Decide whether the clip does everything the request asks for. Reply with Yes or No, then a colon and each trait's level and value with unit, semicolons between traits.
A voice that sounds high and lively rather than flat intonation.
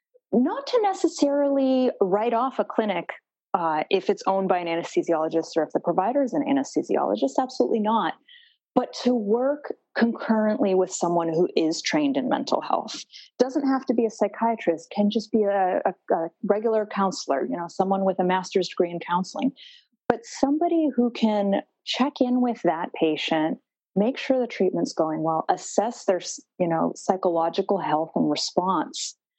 Yes: high, 215 Hz; wide, 6.6 semitones